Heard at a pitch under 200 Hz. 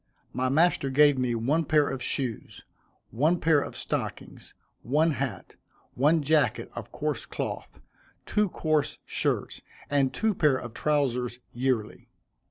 Yes: medium, 140 Hz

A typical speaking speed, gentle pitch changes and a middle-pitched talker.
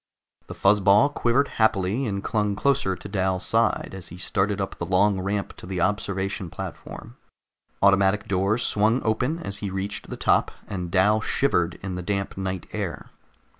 No: average, 170 wpm; narrow, 2.2 semitones; low, 100 Hz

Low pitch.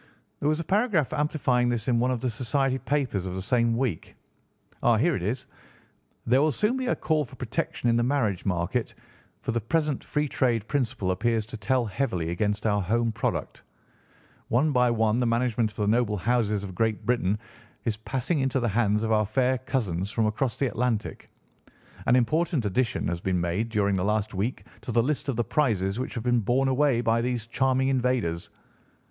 Yes: low, 120 Hz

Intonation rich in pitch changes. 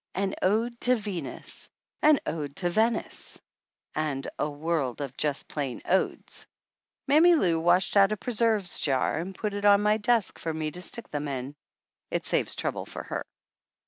Yes: wide, 6.2 semitones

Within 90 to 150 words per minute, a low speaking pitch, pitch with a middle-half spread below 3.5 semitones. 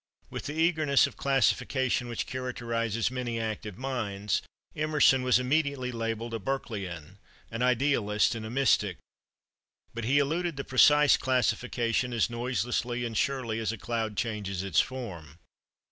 Yes: average, 140 wpm; low, 120 Hz; average, 3.0 semitones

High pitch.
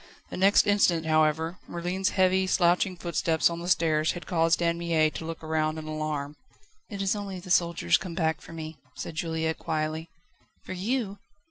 No: medium, 170 Hz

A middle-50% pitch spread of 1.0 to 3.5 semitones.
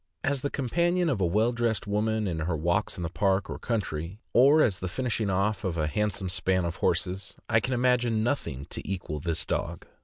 No: average, 5.2 semitones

